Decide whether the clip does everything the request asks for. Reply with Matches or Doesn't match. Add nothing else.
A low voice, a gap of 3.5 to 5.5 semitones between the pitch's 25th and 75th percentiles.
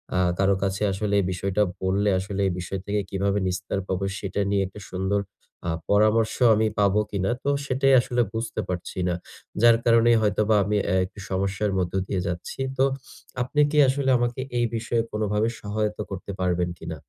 Doesn't match